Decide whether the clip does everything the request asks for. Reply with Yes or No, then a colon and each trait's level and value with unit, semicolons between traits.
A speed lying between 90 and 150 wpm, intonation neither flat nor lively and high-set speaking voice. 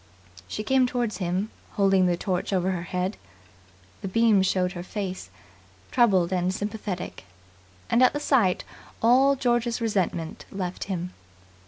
Yes: average, 140 wpm; average, 4.1 semitones; high, 195 Hz